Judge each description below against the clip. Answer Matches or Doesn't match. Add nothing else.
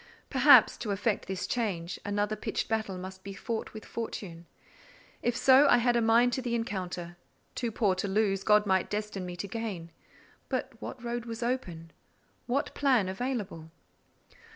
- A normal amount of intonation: Matches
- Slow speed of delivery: Doesn't match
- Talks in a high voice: Matches